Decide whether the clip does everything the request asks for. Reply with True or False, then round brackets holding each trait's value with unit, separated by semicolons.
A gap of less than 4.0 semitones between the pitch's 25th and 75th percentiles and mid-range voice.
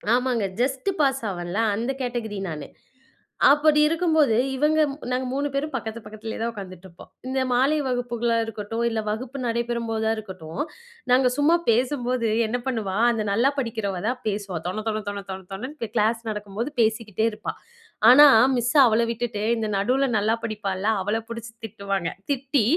False (3.4 semitones; 230 Hz)